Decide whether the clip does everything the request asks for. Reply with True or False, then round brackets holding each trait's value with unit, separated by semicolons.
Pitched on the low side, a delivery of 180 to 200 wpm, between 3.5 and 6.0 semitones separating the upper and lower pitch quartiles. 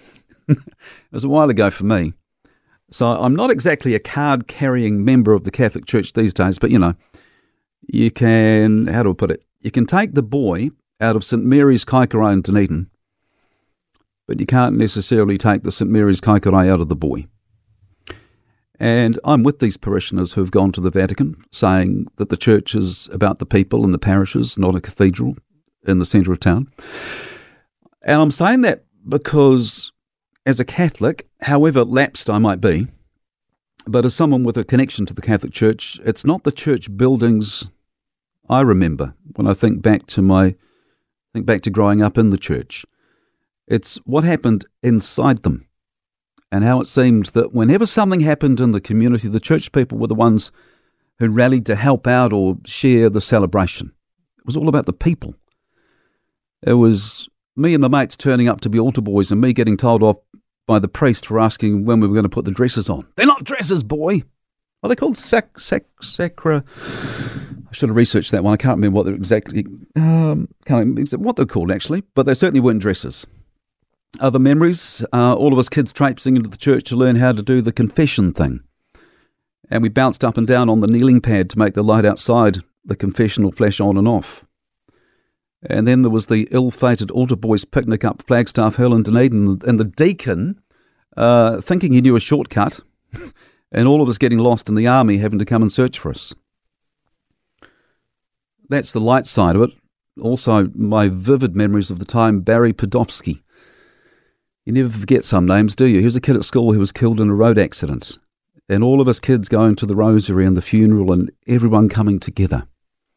True (115 Hz; 190 wpm; 4.1 semitones)